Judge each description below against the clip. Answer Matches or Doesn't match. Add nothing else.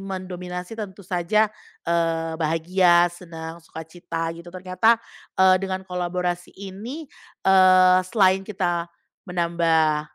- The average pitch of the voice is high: Doesn't match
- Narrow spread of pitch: Matches